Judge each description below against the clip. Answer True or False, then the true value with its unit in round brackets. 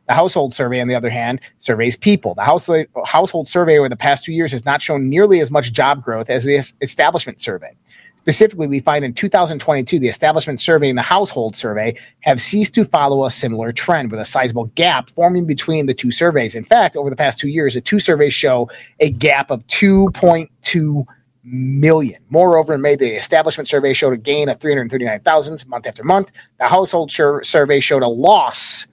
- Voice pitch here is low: False (145 Hz)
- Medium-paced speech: True (195 wpm)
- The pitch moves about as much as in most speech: True (4.2 semitones)